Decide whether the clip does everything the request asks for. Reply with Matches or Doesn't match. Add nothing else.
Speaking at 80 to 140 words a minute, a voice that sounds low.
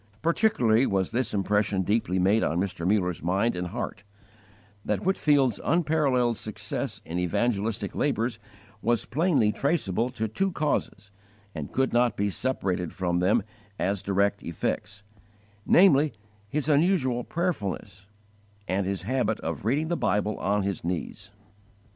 Matches